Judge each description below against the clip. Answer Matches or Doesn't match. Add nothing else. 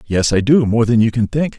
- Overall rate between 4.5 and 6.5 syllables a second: Matches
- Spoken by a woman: Doesn't match